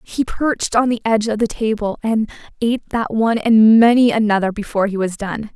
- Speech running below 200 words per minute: No, fast, 205 wpm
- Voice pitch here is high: Yes, high, 220 Hz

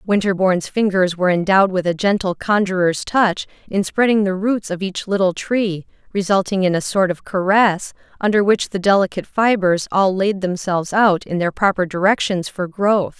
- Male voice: No, female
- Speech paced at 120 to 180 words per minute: Yes, average, 175 wpm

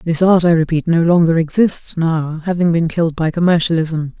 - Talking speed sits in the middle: Yes, average, 185 wpm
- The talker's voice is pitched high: No, medium, 165 Hz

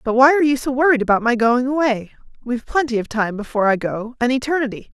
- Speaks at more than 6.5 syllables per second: Yes, 6.7 syllables/s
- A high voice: Yes, high, 245 Hz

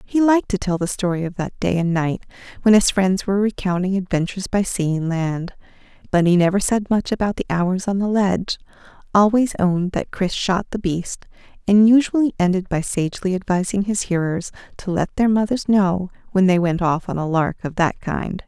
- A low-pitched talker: No, high, 190 Hz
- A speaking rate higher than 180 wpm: Yes, average, 200 wpm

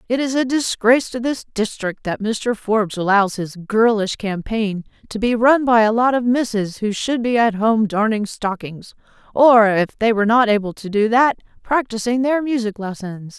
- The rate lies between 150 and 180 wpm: No, average, 190 wpm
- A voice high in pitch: Yes, high, 225 Hz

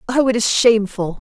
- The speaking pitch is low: No, high, 225 Hz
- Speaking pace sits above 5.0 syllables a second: Yes, 5.8 syllables/s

